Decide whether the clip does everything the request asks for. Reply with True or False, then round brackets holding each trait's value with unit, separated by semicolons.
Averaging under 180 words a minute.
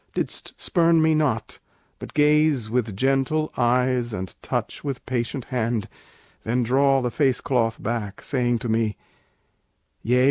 True (140 wpm)